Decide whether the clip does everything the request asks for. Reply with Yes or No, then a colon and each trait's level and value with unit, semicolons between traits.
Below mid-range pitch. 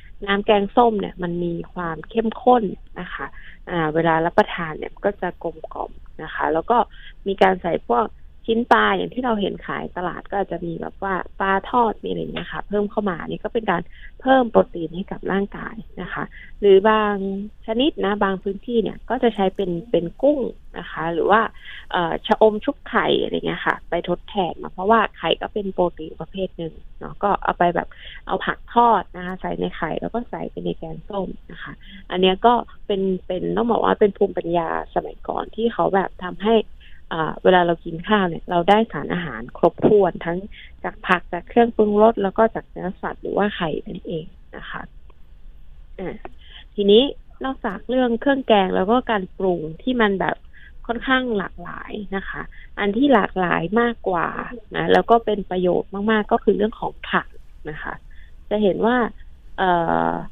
No: high, 200 Hz